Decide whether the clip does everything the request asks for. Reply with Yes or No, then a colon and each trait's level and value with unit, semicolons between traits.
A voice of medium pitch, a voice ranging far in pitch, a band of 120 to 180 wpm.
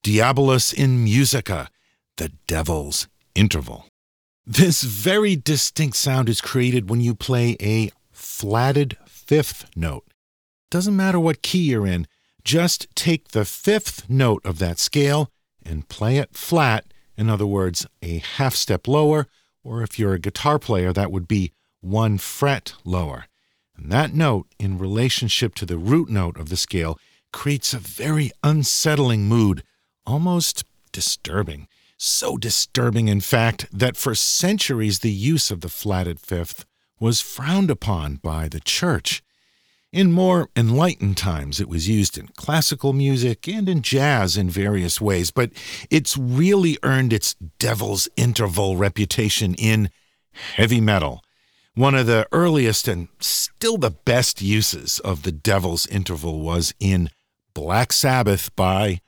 No: low, 110 Hz; wide, 6.7 semitones; average, 140 wpm